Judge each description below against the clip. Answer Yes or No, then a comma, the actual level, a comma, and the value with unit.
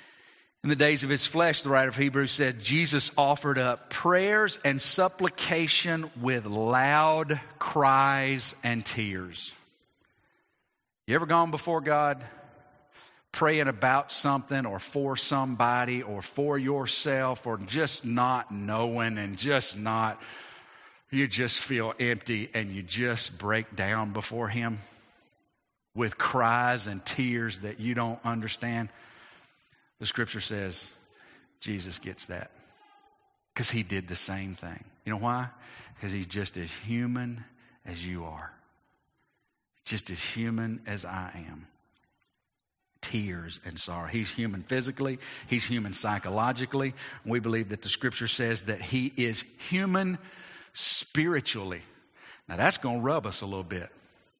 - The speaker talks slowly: Yes, slow, 130 wpm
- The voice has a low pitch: Yes, low, 120 Hz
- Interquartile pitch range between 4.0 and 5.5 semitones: Yes, average, 4.9 semitones